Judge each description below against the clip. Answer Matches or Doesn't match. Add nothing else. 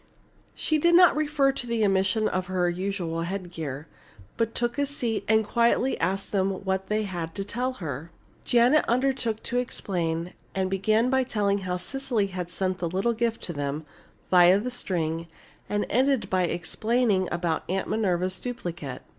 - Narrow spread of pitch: Doesn't match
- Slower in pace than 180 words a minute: Matches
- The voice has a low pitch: Doesn't match